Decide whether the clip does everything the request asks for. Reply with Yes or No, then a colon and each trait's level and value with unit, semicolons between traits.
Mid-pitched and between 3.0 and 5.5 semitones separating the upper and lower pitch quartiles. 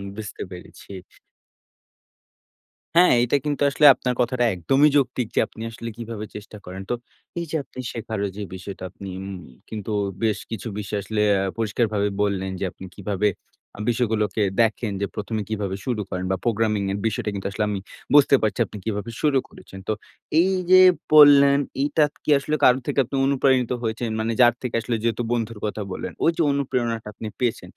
No: low, 110 Hz; average, 3.6 semitones